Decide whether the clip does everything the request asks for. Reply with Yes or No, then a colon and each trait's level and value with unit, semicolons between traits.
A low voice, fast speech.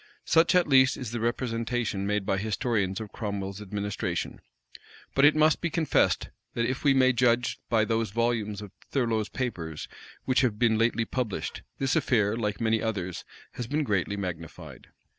No: low, 115 Hz; average, 165 wpm